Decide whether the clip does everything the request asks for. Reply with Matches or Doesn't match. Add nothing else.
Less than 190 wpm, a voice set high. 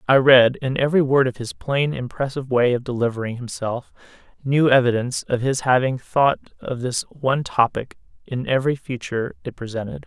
Doesn't match